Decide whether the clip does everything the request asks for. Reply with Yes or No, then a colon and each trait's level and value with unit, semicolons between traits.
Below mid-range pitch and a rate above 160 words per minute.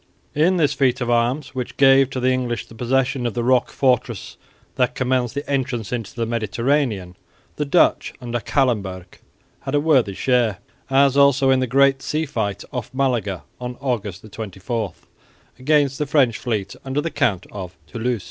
Yes: low, 125 Hz; average, 170 wpm